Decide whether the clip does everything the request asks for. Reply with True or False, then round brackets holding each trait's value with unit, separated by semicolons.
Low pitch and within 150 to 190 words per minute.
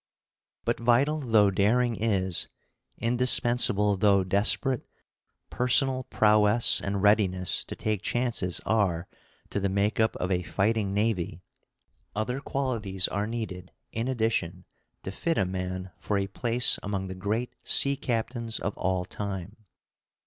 False (105 Hz; 135 wpm)